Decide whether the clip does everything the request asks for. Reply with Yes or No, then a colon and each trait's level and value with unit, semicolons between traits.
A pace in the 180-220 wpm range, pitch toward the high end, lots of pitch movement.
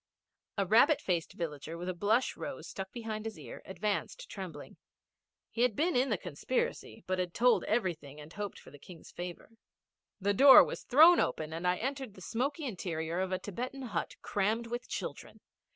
Yes: average, 185 wpm; high, 205 Hz; wide, 5.9 semitones